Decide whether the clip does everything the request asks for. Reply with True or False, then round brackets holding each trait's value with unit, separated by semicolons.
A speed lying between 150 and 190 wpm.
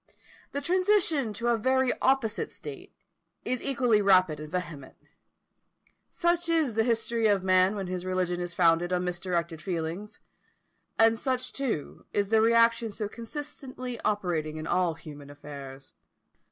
False (140 wpm)